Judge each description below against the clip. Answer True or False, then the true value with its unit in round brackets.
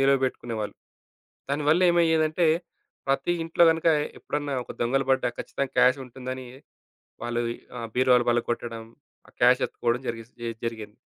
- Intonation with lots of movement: False (3.4 semitones)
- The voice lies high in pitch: False (130 Hz)